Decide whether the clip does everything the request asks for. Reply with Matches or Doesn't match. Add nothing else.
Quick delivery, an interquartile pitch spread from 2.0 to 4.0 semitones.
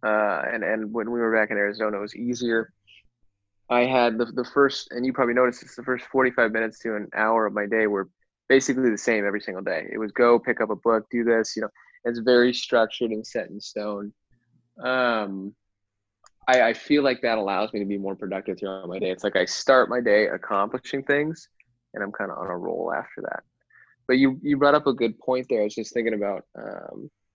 Matches